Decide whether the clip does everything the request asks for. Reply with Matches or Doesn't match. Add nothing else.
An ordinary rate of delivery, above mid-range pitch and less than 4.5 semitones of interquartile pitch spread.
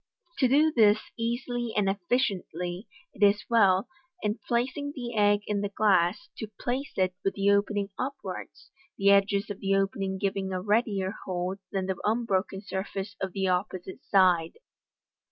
Matches